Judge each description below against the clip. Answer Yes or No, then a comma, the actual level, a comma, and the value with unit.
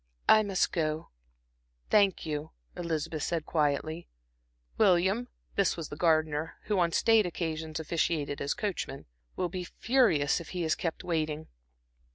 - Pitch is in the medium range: Yes, medium, 165 Hz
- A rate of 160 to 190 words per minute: No, average, 140 wpm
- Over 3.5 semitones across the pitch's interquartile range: No, average, 2.9 semitones